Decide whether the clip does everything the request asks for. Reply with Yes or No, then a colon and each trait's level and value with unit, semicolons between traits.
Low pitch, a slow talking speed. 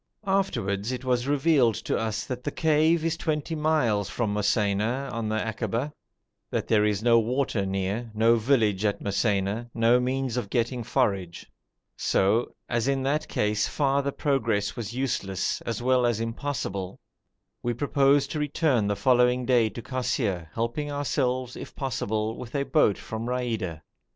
No: low, 120 Hz; average, 155 wpm